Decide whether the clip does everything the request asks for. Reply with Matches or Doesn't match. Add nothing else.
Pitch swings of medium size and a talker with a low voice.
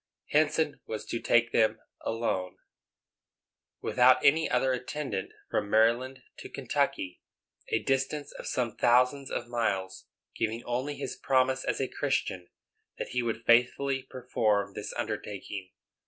Matches